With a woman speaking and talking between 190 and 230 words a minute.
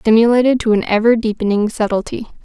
No: female; average, 150 wpm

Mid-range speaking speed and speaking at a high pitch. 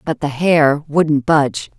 No: average, 170 wpm; medium, 150 Hz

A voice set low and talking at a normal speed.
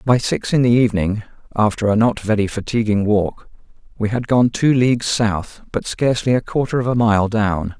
Yes: low, 110 Hz; average, 190 wpm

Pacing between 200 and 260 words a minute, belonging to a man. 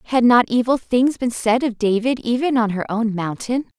No: fast, 205 wpm; female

